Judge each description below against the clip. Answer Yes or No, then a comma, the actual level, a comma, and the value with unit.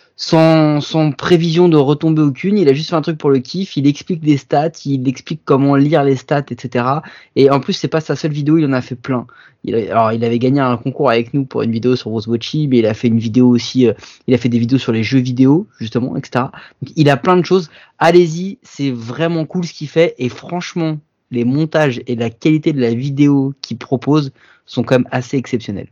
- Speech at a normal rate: No, fast, 240 wpm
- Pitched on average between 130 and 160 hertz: Yes, medium, 140 Hz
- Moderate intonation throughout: Yes, average, 4.2 semitones